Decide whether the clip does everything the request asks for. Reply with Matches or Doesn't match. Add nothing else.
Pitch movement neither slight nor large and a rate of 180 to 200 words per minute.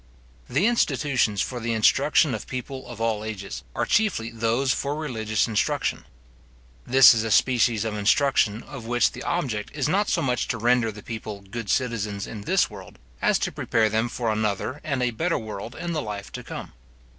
Matches